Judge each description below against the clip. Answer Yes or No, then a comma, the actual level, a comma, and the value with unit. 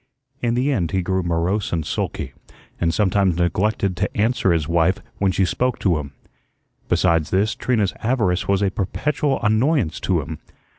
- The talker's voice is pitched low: Yes, very low, 95 Hz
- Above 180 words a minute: No, average, 165 wpm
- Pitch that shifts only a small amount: No, average, 4.2 semitones